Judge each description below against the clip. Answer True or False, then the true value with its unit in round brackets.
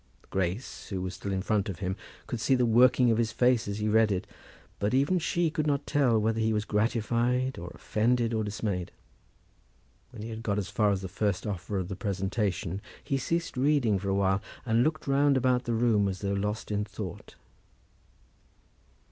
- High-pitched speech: False (110 Hz)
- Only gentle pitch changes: False (3.9 semitones)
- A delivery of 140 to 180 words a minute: False (200 wpm)